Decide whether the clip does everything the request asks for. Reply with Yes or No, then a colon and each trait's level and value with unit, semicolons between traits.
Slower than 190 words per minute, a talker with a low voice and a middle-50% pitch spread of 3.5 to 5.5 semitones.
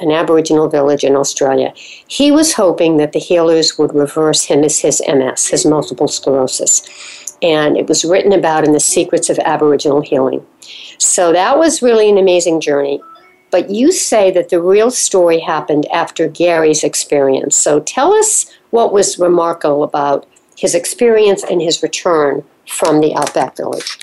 No: average, 160 wpm; medium, 165 Hz; average, 3.9 semitones